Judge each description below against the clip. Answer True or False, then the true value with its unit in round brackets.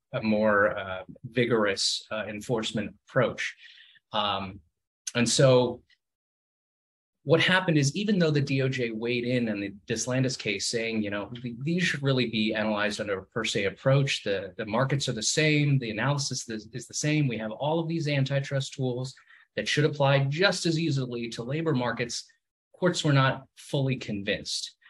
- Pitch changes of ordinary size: True (4.8 semitones)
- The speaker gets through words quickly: False (165 wpm)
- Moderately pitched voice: False (125 Hz)